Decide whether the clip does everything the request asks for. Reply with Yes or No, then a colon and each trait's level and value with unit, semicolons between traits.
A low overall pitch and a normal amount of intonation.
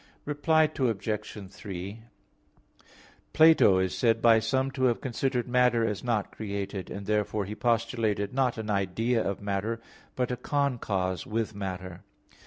Yes: low, 110 Hz; average, 3.9 semitones